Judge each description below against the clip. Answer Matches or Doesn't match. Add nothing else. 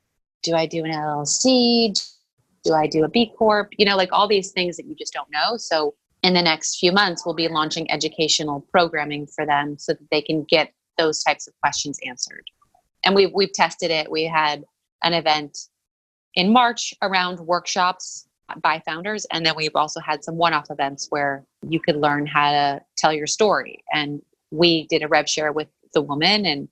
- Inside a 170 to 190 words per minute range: Doesn't match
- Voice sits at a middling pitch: Matches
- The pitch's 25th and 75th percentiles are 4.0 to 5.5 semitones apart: Doesn't match